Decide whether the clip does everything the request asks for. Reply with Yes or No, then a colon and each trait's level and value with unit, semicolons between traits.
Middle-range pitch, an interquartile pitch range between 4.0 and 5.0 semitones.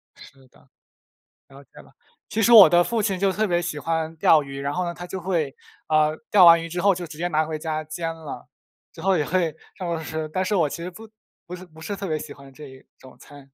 No: medium, 165 Hz; average, 3.0 semitones